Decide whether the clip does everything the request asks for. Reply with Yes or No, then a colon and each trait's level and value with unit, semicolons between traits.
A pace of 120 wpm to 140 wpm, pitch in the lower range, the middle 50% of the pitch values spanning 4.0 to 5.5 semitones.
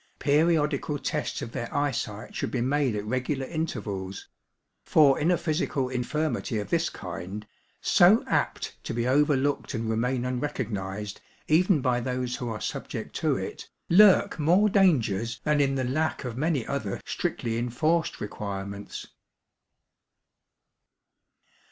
Yes: slow, 135 wpm; low, 130 Hz; average, 5.0 semitones